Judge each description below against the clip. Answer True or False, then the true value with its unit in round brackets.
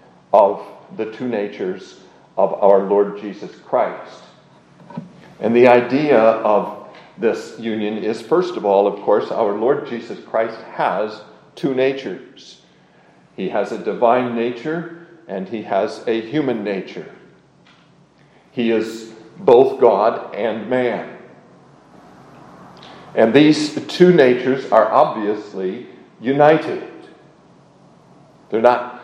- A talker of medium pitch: False (120 Hz)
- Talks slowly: True (110 wpm)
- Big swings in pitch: False (4.3 semitones)